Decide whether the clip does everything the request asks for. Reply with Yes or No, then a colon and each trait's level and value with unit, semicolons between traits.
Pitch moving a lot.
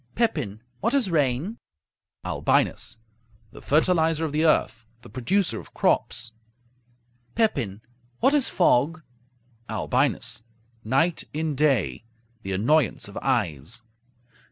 Yes: wide, 6.3 semitones